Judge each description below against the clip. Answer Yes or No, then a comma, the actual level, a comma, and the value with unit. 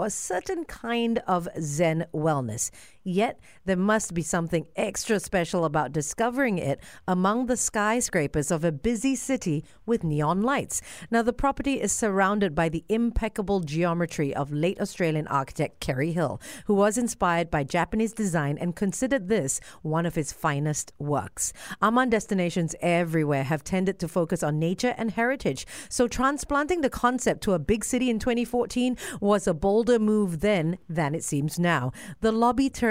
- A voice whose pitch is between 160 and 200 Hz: Yes, high, 190 Hz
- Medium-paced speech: Yes, average, 160 wpm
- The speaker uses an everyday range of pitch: No, wide, 5.9 semitones